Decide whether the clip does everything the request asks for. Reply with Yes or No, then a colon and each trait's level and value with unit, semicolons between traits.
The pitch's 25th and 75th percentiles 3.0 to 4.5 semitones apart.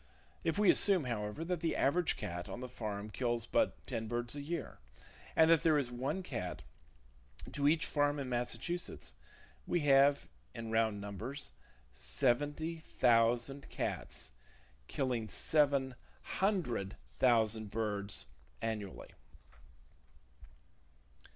No: average, 5.1 semitones